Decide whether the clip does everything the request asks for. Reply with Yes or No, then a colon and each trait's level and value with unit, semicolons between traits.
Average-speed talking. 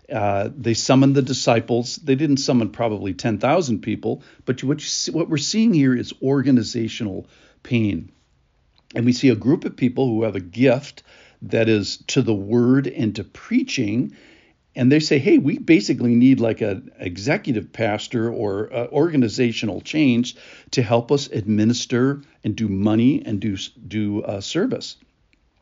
Yes: average, 155 wpm